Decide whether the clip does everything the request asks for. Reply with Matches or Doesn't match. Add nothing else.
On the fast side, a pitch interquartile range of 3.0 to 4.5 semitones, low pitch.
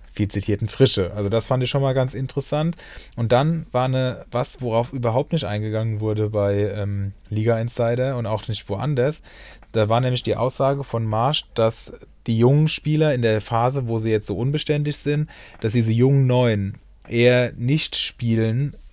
Doesn't match